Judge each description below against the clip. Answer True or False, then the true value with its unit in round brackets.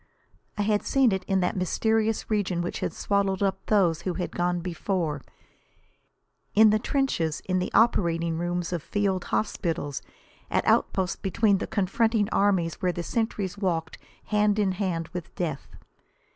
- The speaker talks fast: False (155 wpm)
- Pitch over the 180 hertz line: True (190 Hz)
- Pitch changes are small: False (3.1 semitones)